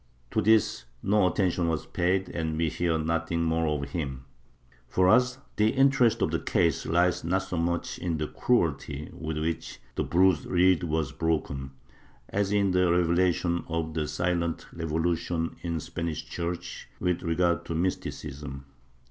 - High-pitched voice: No, very low, 85 Hz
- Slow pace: No, average, 160 wpm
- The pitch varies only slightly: Yes, narrow, 2.2 semitones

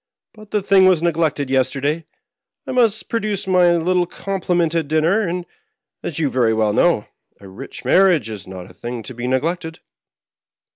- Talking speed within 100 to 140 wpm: No, average, 175 wpm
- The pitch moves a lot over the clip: Yes, wide, 6.0 semitones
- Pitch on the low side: No, medium, 165 Hz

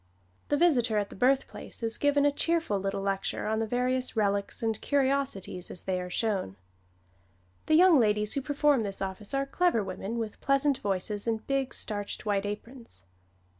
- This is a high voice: Yes, high, 225 Hz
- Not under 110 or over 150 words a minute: No, average, 170 wpm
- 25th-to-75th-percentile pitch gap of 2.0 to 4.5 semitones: No, average, 5.3 semitones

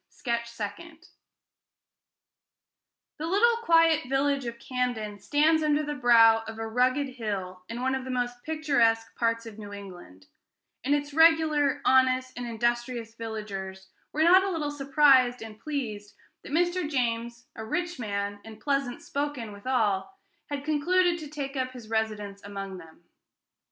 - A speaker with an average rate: Yes, average, 150 wpm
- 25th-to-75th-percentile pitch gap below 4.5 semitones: No, average, 4.8 semitones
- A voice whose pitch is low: No, very high, 250 Hz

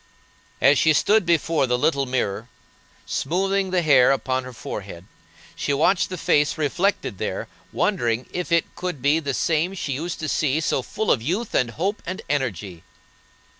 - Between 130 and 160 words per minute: No, average, 170 wpm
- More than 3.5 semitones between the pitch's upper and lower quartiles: Yes, wide, 5.5 semitones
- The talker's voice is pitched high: No, medium, 145 Hz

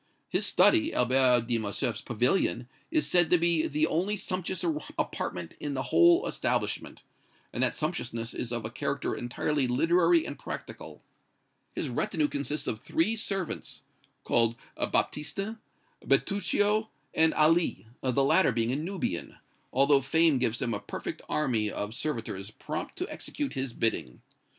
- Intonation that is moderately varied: No, wide, 6.5 semitones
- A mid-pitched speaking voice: Yes, medium, 150 Hz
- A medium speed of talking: Yes, average, 145 wpm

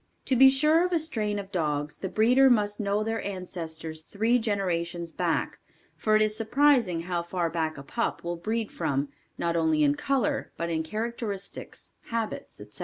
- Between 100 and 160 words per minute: No, average, 180 wpm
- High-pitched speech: Yes, high, 200 Hz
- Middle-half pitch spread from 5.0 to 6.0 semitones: Yes, wide, 5.4 semitones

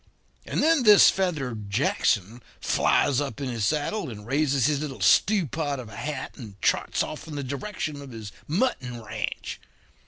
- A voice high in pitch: No, medium, 140 Hz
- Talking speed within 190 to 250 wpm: No, average, 165 wpm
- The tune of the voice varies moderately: Yes, average, 4.5 semitones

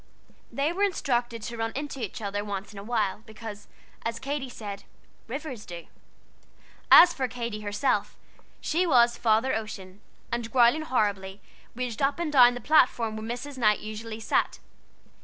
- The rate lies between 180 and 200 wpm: No, average, 160 wpm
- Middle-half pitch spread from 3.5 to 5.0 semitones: Yes, average, 3.8 semitones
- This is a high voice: Yes, high, 230 Hz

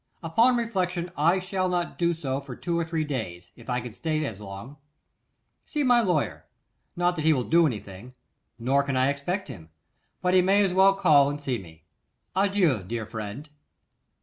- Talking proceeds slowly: No, average, 185 wpm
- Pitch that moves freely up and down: Yes, wide, 6.6 semitones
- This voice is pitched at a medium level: Yes, medium, 155 Hz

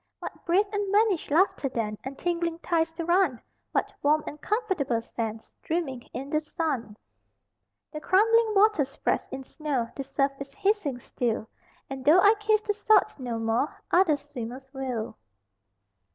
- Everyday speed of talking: Yes, average, 155 wpm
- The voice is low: No, very high, 300 Hz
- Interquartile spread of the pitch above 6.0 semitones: Yes, wide, 6.8 semitones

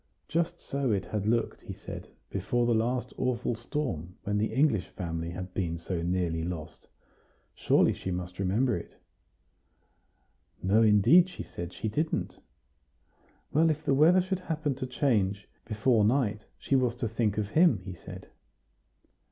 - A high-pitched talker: No, low, 110 Hz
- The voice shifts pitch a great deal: Yes, wide, 6.3 semitones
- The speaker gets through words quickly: No, average, 155 wpm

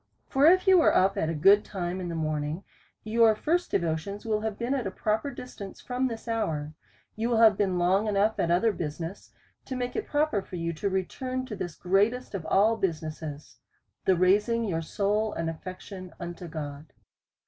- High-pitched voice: Yes, high, 200 Hz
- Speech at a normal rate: Yes, average, 190 wpm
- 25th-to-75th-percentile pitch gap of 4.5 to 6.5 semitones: Yes, average, 4.9 semitones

